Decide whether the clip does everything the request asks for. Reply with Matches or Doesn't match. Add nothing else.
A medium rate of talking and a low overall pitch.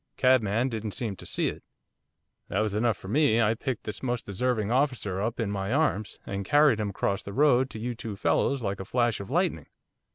Doesn't match